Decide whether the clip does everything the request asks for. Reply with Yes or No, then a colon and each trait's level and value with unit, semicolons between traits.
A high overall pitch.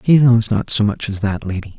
No: low, 110 Hz